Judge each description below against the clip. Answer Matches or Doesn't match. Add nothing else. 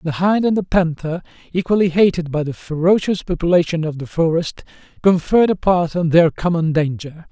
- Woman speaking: Doesn't match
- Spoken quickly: Doesn't match